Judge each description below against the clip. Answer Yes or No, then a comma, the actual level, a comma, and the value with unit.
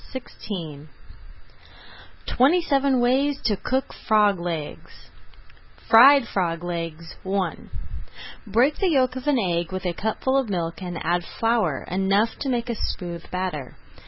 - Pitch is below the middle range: No, high, 200 Hz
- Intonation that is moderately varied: No, wide, 6.7 semitones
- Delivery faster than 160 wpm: No, average, 140 wpm